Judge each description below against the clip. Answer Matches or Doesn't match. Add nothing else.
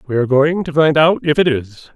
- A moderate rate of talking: Doesn't match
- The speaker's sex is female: Doesn't match